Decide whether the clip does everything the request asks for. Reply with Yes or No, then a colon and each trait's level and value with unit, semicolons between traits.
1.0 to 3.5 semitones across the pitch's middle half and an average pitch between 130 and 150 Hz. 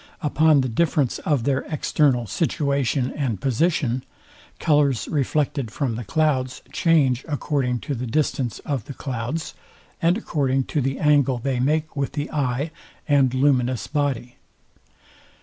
Yes: average, 3.0 semitones; medium, 140 Hz